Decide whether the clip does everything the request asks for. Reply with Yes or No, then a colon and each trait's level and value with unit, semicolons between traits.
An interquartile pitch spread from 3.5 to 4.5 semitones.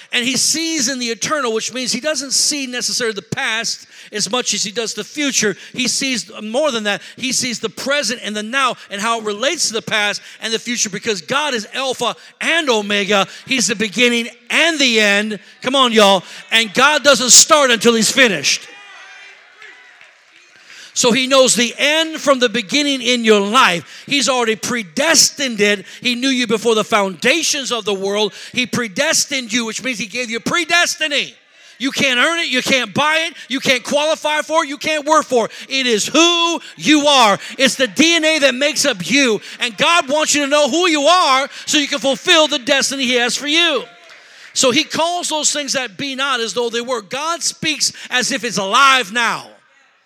Yes: average, 4.2 semitones